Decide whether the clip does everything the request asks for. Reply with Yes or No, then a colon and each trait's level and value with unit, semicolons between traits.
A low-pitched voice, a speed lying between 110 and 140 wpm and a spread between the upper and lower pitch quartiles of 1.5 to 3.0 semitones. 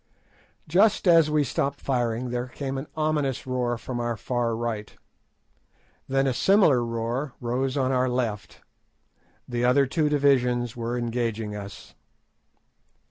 Yes: low, 125 Hz; slow, 135 wpm; average, 2.7 semitones